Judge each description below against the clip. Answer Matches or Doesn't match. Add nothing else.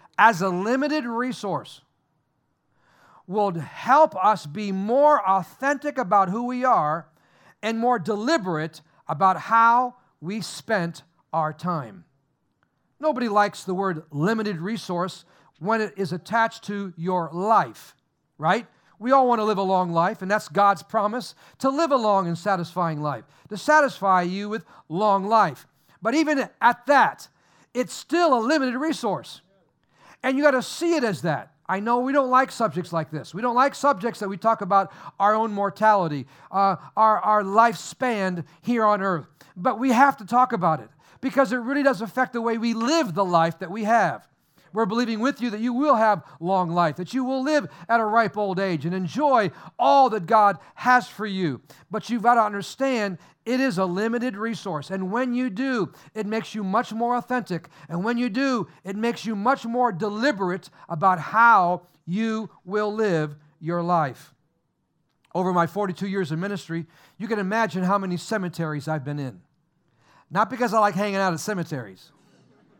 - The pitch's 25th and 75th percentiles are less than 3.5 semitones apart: Doesn't match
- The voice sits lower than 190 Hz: Doesn't match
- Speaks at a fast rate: Doesn't match